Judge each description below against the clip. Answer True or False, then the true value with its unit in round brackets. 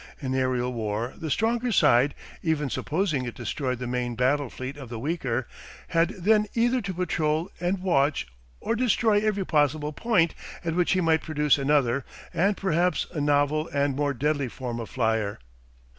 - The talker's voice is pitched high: False (150 Hz)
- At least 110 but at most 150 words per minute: False (170 wpm)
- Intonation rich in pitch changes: True (5.8 semitones)